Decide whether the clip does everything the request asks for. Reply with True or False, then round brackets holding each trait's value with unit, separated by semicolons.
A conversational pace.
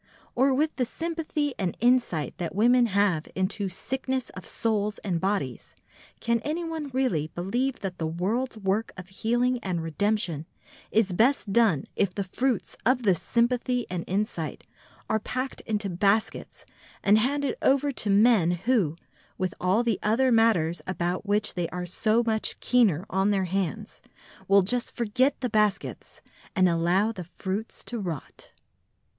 True (150 wpm)